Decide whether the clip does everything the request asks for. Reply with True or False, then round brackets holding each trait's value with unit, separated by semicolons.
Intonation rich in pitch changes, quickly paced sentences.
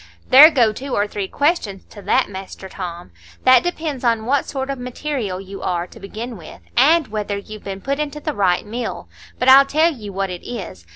True (5.9 semitones; 210 wpm)